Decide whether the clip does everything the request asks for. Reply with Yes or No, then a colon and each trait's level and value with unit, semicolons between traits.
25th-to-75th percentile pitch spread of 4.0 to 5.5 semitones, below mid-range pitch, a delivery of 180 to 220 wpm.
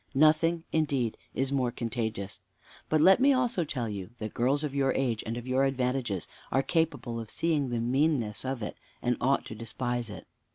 Yes: average, 4.3 semitones; low, 130 Hz; average, 190 wpm